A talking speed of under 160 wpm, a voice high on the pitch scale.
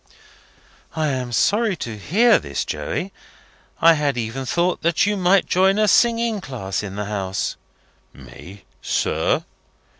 No: average, 140 wpm; medium, 160 Hz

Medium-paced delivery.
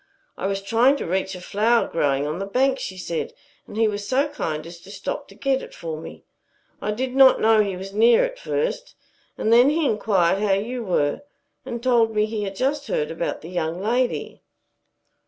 No: fast, 210 wpm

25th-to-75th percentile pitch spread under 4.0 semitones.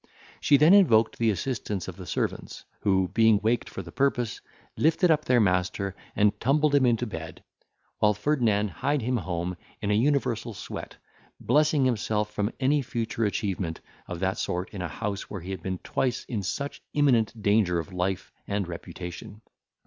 No: average, 5.1 semitones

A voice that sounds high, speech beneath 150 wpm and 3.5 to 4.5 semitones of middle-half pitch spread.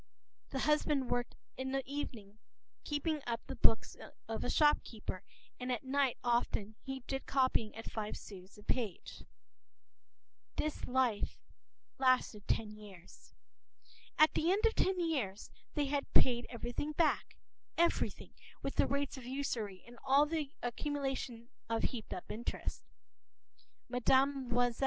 Yes: very high, 260 Hz; average, 140 wpm; average, 3.8 semitones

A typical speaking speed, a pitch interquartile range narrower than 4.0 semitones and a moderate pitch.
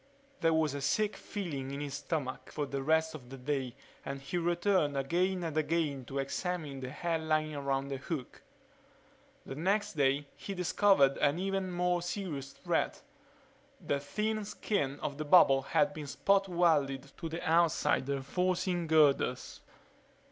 No: average, 155 wpm; average, 4.4 semitones; medium, 155 Hz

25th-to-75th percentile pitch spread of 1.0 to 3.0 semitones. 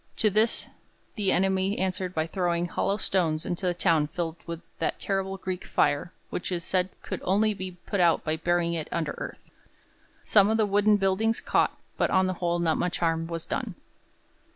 Yes: narrow, 2.4 semitones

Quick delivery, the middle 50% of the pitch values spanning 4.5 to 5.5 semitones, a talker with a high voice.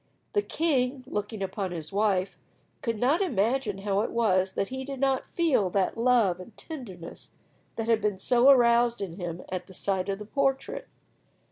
No: average, 170 wpm; average, 5.1 semitones; high, 220 Hz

